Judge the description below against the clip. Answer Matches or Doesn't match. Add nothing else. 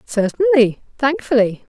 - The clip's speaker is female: Matches